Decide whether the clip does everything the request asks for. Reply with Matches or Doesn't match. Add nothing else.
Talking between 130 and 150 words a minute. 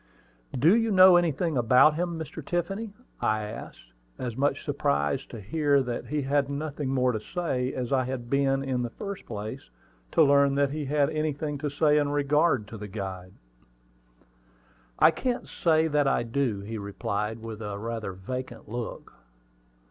Doesn't match